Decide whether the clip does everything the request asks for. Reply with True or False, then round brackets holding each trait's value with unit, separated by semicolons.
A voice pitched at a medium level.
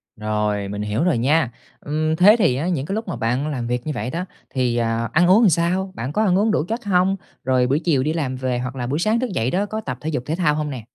True (150 Hz)